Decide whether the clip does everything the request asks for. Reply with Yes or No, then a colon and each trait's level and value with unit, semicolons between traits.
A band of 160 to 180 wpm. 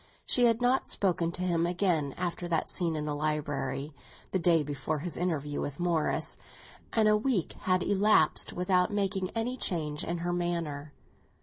Yes: average, 170 wpm